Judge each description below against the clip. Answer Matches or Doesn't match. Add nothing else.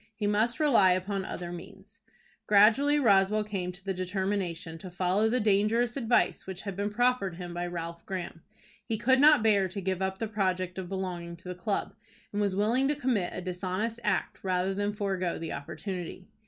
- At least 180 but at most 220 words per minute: Matches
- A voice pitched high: Matches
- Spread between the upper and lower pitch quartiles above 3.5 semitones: Doesn't match